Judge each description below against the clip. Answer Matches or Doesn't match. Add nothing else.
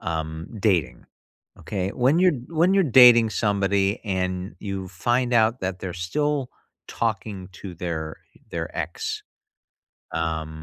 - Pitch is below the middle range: Matches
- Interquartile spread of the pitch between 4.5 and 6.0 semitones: Matches